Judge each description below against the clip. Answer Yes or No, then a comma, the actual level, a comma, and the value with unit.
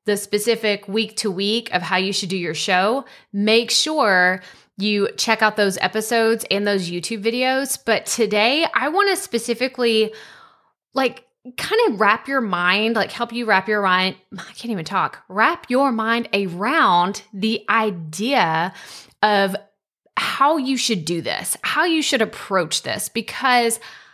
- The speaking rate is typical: Yes, average, 155 wpm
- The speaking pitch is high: Yes, high, 220 Hz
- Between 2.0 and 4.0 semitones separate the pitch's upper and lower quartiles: Yes, average, 3.3 semitones